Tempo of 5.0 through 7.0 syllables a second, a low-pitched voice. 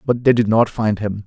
Yes: 5.1 syllables/s; low, 110 Hz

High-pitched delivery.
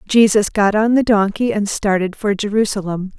Yes: high, 205 Hz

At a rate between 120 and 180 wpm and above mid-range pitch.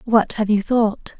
No: average, 200 wpm; high, 215 Hz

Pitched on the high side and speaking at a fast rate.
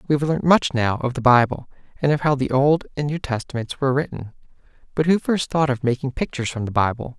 No: low, 135 Hz; fast, 235 wpm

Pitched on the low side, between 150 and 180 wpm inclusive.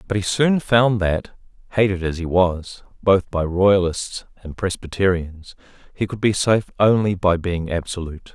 Yes: very low, 95 Hz; average, 160 wpm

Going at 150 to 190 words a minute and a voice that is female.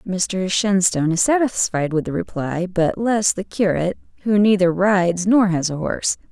Yes: average, 170 wpm; female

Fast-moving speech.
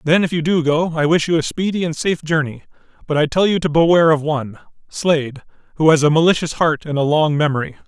Yes: fast, 235 wpm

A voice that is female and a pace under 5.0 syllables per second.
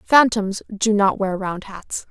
Yes: female; 3.6 syllables/s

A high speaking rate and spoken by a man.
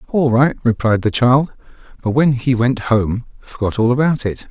No: average, 185 wpm; male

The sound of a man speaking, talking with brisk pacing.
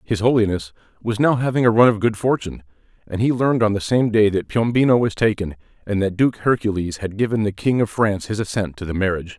Yes: male; fast, 230 wpm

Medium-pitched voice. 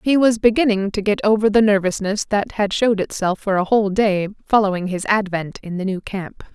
No: high, 205 Hz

